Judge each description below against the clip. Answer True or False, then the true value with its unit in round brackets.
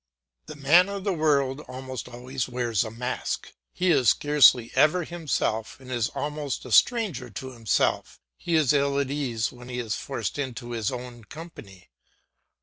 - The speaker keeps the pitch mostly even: False (3.7 semitones)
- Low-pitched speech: True (130 Hz)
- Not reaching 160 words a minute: False (165 wpm)